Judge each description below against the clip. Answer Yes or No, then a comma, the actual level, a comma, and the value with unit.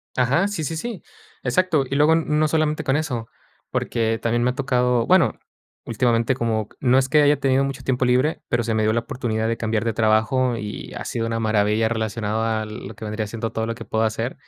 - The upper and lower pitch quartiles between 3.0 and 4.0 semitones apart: Yes, average, 3.5 semitones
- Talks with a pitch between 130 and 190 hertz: No, low, 120 Hz